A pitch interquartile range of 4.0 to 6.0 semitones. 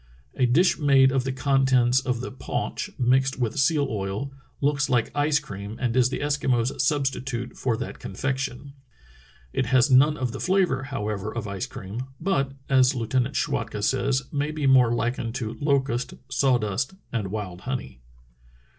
No: narrow, 2.6 semitones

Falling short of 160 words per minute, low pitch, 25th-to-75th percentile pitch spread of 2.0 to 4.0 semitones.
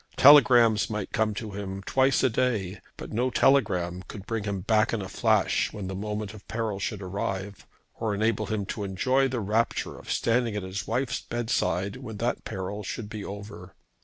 No: average, 190 wpm; low, 105 Hz; average, 2.8 semitones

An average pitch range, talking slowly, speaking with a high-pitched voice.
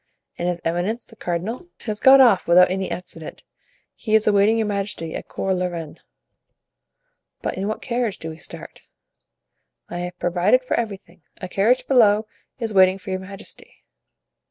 No: average, 3.8 semitones; average, 165 wpm; high, 195 Hz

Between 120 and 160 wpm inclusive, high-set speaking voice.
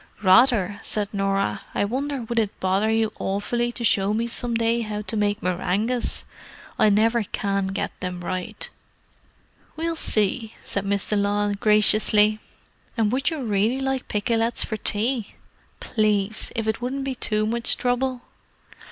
Yes: average, 150 wpm; high, 215 Hz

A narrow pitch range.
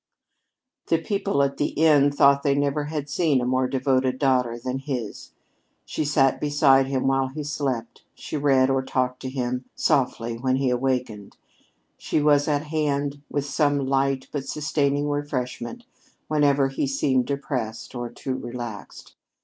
Yes: narrow, 2.1 semitones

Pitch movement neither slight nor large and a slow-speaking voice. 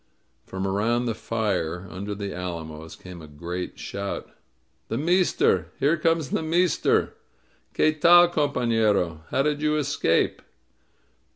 No: wide, 9.0 semitones; slow, 130 wpm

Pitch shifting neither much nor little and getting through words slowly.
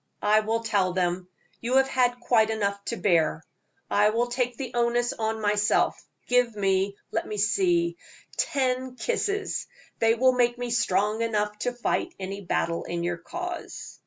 No: average, 3.5 semitones; average, 160 wpm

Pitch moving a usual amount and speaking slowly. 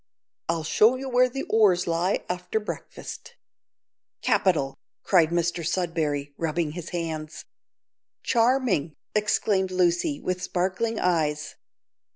Yes: average, 4.3 semitones; slow, 110 wpm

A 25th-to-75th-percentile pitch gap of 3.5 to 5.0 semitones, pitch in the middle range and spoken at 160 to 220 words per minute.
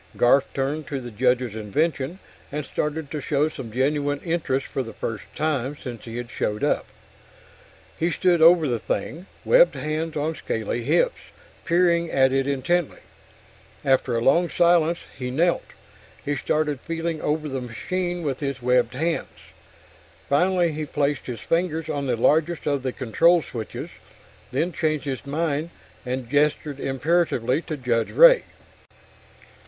No: average, 4.2 semitones; medium, 145 Hz; average, 150 wpm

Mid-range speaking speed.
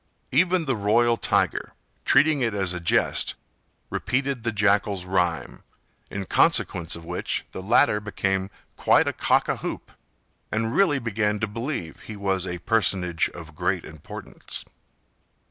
Yes: average, 145 wpm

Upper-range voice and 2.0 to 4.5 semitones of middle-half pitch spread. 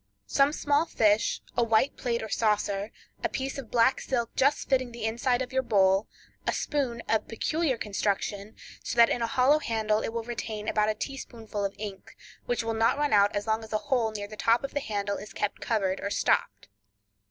Yes: high, 225 Hz; average, 3.3 semitones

